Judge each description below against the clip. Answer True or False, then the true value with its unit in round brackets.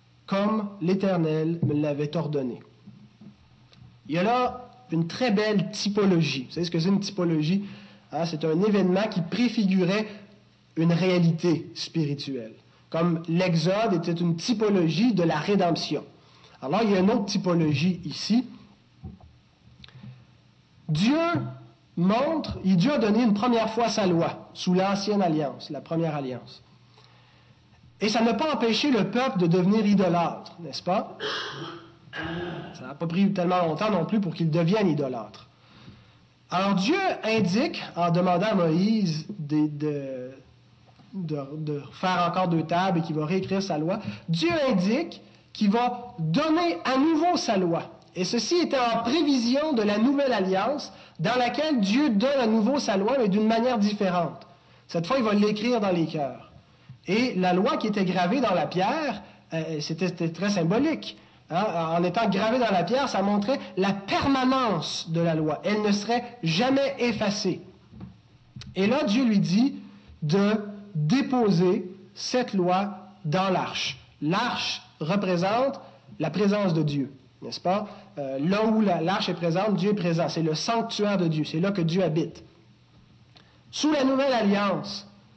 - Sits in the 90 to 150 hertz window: False (185 Hz)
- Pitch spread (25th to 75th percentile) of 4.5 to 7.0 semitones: True (5.0 semitones)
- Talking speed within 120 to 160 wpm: True (155 wpm)